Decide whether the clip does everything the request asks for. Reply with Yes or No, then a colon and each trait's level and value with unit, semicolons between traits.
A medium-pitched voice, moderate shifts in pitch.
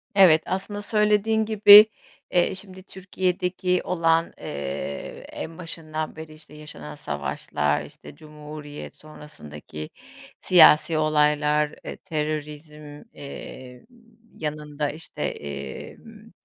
Yes: medium, 155 Hz; average, 3.6 semitones